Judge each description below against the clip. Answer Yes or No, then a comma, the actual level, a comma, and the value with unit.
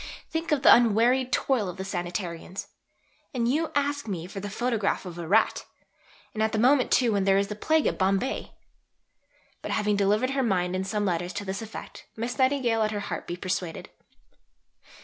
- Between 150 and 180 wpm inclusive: No, average, 190 wpm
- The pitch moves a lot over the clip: No, average, 4.7 semitones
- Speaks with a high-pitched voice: Yes, high, 210 Hz